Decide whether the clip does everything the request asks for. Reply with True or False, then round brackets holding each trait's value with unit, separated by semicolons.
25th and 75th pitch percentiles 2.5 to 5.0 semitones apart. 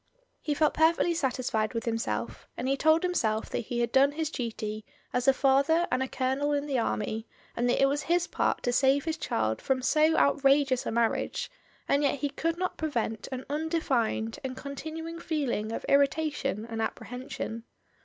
True (4.7 semitones)